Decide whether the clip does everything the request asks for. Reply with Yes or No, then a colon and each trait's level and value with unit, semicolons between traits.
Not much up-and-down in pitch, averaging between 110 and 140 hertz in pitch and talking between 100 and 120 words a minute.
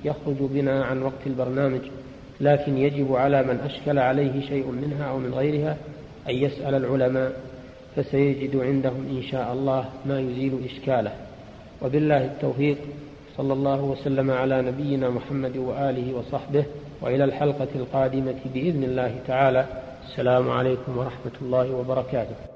No: narrow, 1.4 semitones; low, 135 Hz; average, 130 wpm